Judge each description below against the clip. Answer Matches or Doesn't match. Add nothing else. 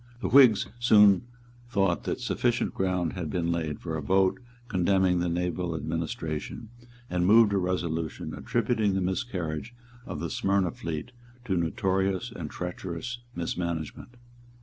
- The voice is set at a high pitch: Doesn't match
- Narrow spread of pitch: Doesn't match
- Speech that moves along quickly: Doesn't match